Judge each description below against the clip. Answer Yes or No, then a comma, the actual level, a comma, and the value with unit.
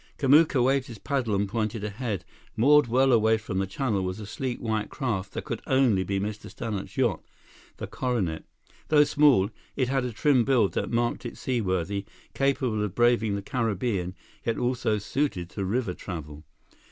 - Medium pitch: No, low, 115 Hz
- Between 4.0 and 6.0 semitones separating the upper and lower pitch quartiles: Yes, average, 4.6 semitones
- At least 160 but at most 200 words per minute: Yes, average, 175 wpm